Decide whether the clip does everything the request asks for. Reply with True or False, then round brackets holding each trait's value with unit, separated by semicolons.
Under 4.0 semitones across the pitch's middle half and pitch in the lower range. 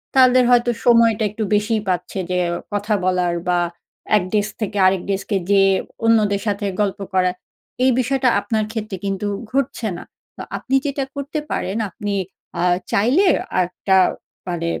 False (3.6 semitones; 210 Hz)